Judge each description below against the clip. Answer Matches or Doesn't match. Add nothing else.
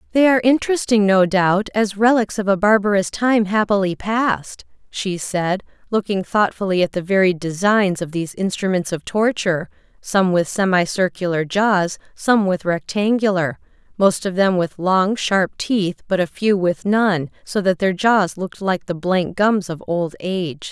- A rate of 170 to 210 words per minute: Doesn't match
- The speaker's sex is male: Doesn't match